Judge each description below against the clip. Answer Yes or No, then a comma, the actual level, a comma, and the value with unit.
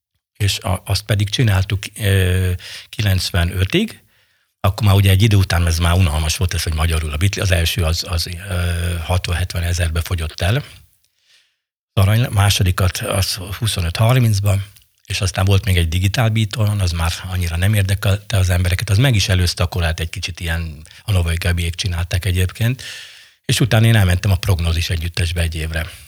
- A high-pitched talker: No, very low, 95 Hz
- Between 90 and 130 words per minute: No, fast, 155 wpm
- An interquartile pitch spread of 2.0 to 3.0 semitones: Yes, average, 2.7 semitones